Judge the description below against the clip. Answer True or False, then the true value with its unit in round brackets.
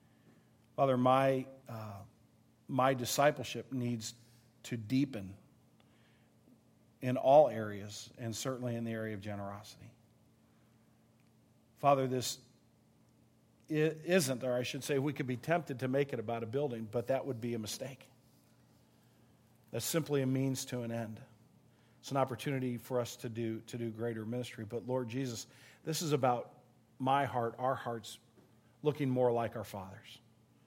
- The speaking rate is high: False (145 wpm)